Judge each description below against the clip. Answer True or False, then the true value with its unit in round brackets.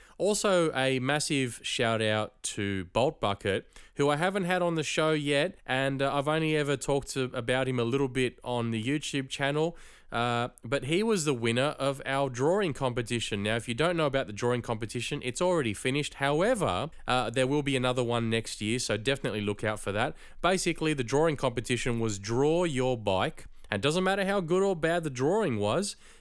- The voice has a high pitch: False (135 Hz)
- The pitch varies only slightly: False (4.5 semitones)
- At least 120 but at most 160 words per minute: False (200 wpm)